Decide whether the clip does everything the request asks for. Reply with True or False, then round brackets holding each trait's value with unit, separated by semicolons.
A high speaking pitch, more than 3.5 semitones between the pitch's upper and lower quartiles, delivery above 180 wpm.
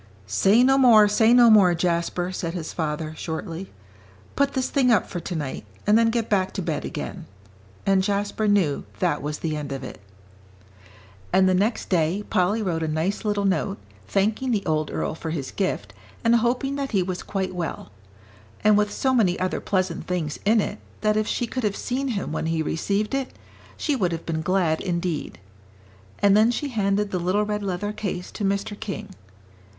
True (195 Hz; 4.1 semitones; 190 wpm)